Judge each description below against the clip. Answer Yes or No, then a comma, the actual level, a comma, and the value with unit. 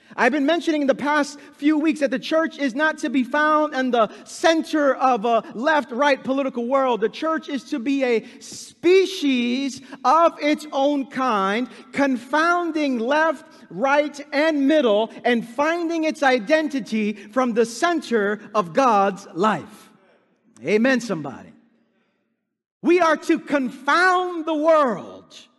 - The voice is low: No, very high, 280 Hz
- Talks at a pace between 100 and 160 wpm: Yes, average, 140 wpm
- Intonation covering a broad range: No, average, 4.1 semitones